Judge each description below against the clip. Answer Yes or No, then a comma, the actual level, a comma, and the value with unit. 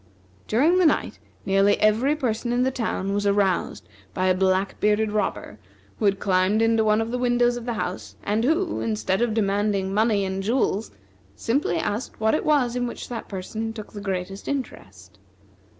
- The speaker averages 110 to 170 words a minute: No, average, 180 wpm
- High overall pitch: Yes, high, 215 Hz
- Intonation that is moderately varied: Yes, average, 3.7 semitones